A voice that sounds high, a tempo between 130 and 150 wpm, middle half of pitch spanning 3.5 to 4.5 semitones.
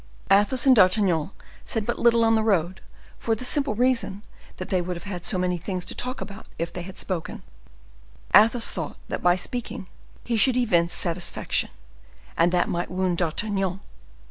No: high, 195 Hz; average, 175 wpm; average, 4.2 semitones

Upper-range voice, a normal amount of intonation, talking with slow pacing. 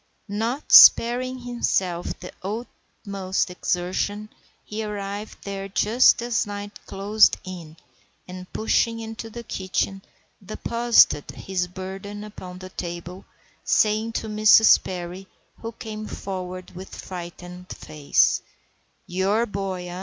Yes: high, 195 Hz; average, 3.0 semitones; slow, 115 wpm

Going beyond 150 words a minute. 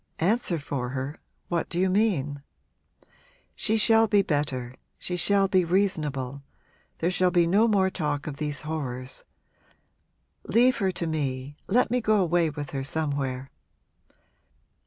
No: average, 140 wpm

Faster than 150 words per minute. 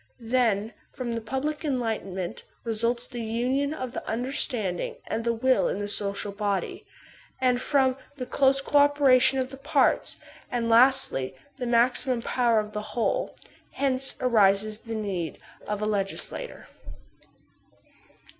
No: average, 145 wpm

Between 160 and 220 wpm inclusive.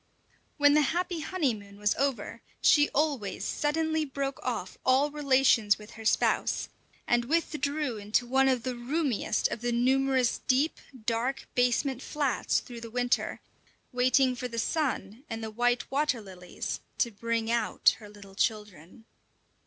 No: average, 145 wpm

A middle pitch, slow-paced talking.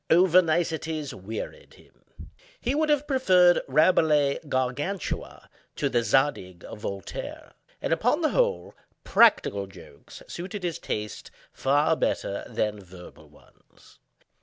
Yes: medium, 145 Hz; slow, 120 wpm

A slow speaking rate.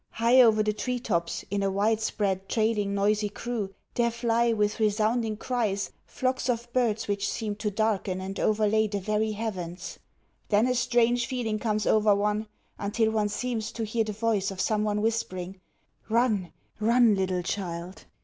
No: average, 165 wpm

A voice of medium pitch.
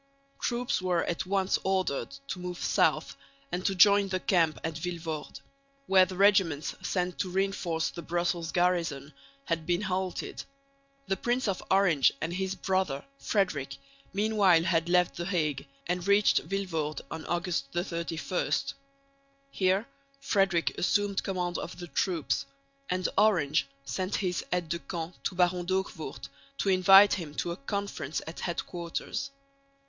Yes: medium, 180 Hz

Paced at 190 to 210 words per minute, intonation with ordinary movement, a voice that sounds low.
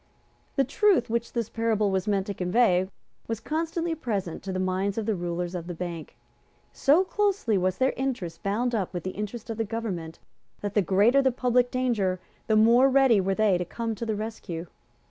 No: average, 200 wpm; average, 4.7 semitones; high, 215 Hz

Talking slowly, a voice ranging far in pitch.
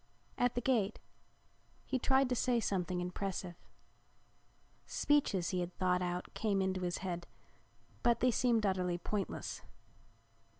No: slow, 130 wpm; average, 4.8 semitones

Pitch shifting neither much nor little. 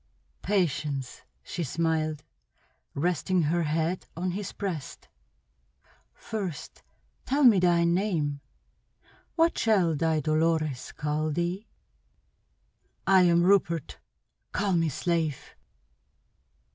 Yes: average, 3.1 semitones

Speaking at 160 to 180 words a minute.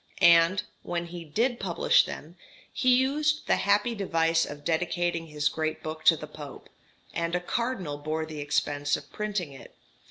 Yes: average, 165 wpm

